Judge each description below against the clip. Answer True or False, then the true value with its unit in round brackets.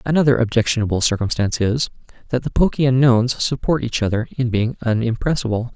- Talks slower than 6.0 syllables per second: False (6.1 syllables/s)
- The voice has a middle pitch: False (120 Hz)